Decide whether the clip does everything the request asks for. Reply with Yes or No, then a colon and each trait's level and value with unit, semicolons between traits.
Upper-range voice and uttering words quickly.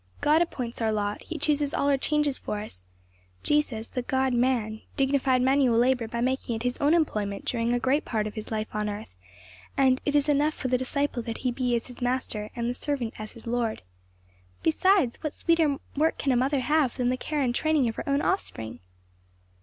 Yes: very high, 255 Hz; fast, 210 wpm